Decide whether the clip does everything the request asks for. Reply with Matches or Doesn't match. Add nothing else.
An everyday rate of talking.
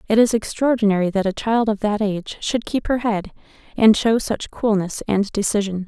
Matches